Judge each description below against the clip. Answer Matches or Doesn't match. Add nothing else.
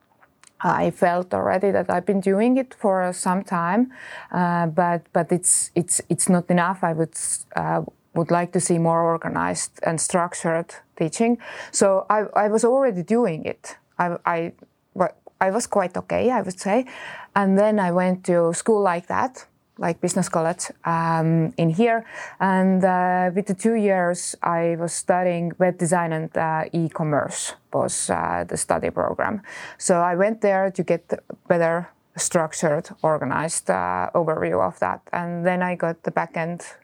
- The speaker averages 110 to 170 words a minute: Matches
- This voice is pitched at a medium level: Matches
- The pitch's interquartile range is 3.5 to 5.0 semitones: Doesn't match